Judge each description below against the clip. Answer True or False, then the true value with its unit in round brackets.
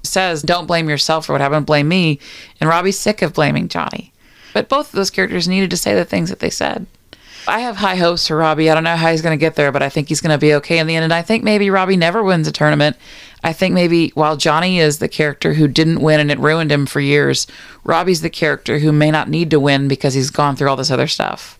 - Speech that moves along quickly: True (270 wpm)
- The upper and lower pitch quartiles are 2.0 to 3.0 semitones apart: True (2.6 semitones)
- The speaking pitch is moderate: True (160 Hz)